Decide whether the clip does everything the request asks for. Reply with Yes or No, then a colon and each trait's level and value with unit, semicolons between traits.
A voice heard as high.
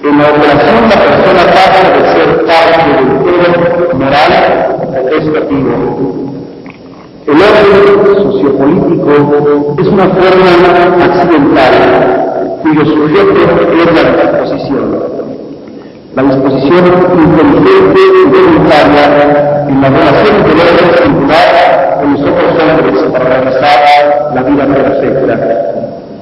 No: medium, 155 Hz